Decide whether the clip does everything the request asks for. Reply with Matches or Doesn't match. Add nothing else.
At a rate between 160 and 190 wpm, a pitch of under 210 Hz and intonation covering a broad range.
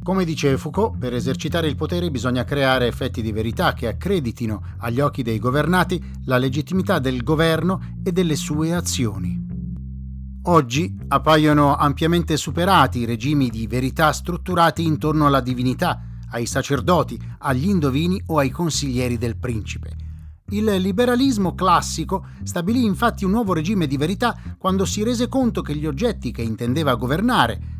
Doesn't match